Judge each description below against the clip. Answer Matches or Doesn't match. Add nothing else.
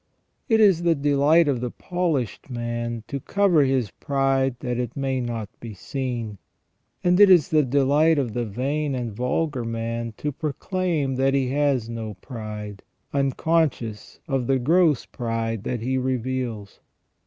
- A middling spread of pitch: Matches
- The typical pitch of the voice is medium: Doesn't match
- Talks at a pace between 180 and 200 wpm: Doesn't match